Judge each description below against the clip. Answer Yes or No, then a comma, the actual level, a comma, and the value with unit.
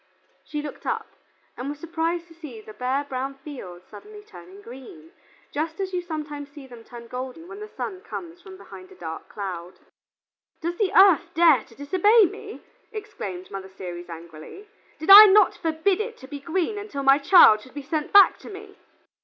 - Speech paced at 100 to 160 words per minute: No, average, 185 wpm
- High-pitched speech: Yes, very high, 305 Hz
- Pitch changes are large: Yes, wide, 7.0 semitones